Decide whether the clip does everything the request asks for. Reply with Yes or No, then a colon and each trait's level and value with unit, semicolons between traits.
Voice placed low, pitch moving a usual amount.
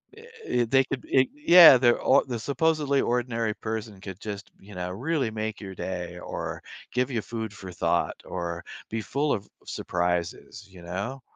No: low, 110 Hz; wide, 5.7 semitones